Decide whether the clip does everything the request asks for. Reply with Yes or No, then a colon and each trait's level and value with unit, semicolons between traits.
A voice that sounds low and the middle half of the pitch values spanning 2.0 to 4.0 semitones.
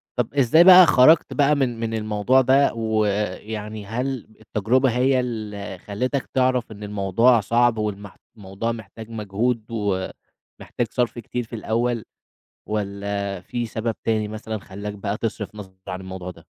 Yes: low, 110 Hz; average, 3.1 semitones